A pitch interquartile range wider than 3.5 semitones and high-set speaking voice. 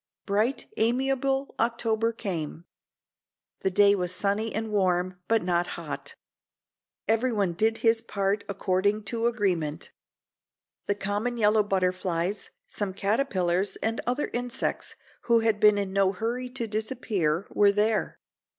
No: average, 3.2 semitones; high, 210 Hz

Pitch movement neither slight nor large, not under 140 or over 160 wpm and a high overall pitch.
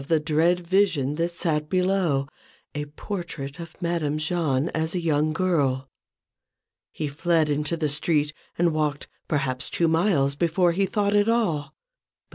No: average, 3.0 semitones; average, 150 wpm; medium, 160 Hz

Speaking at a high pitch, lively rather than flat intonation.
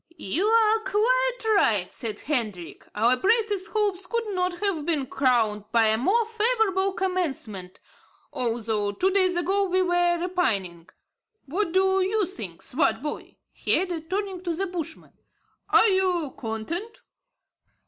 Yes: very high, 360 Hz; wide, 8.5 semitones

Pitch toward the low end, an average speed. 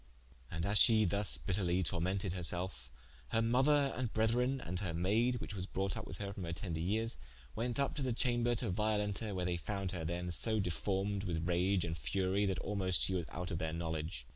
No: very low, 95 Hz; fast, 215 wpm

